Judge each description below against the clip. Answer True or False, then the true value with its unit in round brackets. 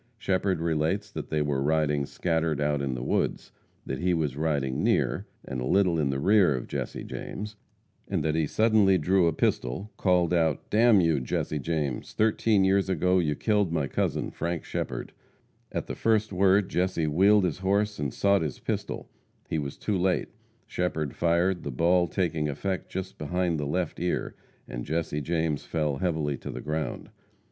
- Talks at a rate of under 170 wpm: False (175 wpm)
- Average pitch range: True (4.1 semitones)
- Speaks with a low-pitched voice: True (85 Hz)